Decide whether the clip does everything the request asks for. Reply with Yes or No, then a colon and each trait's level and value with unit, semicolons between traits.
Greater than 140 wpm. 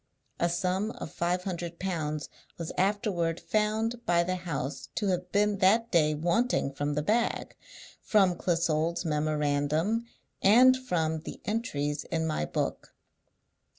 No: slow, 135 wpm